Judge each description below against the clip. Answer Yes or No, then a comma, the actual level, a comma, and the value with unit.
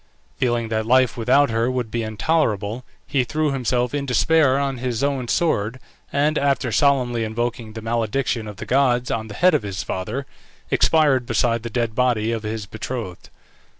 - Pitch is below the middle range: Yes, low, 120 Hz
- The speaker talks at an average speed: Yes, average, 175 wpm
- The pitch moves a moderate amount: Yes, average, 3.5 semitones